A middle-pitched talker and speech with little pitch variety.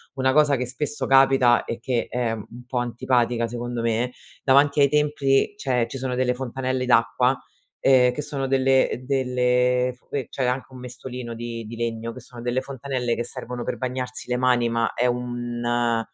No: low, 125 Hz; narrow, 1.7 semitones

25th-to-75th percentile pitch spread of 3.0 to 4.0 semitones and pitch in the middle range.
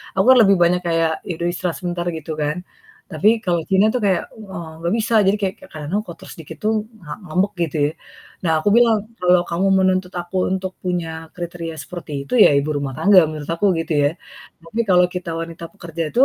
No: narrow, 2.4 semitones; medium, 175 Hz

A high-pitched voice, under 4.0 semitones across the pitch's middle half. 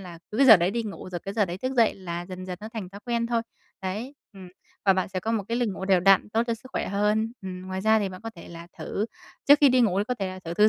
Yes: high, 200 Hz; average, 3.5 semitones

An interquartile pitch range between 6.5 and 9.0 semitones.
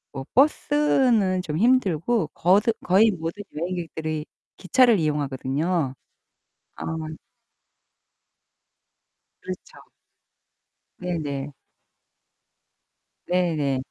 No: average, 5.2 semitones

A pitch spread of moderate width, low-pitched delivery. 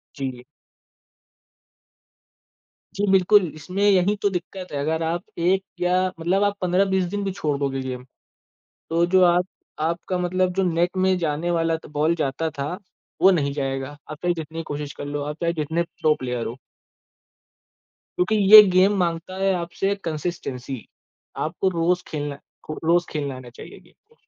No: average, 3.9 semitones; medium, 170 Hz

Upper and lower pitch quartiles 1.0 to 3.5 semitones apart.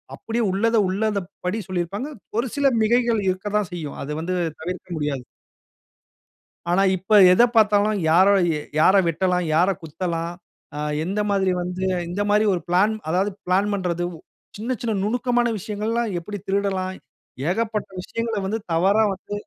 Yes: average, 3.2 semitones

